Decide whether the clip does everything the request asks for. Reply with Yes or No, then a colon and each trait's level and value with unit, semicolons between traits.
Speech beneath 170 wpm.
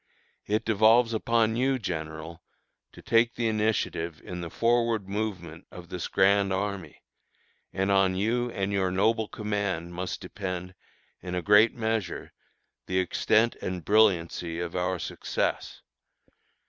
Yes: slow, 135 wpm